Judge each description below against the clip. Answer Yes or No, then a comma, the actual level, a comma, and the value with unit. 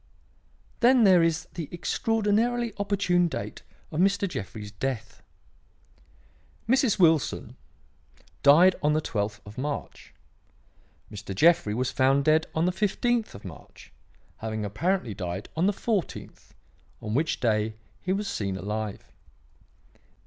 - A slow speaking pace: Yes, slow, 125 wpm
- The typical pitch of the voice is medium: Yes, medium, 155 Hz